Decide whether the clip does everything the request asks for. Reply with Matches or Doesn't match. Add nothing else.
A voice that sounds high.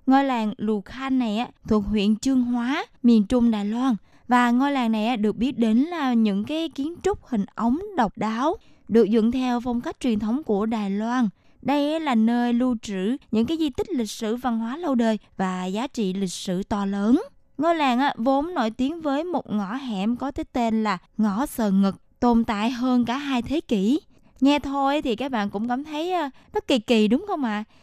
Matches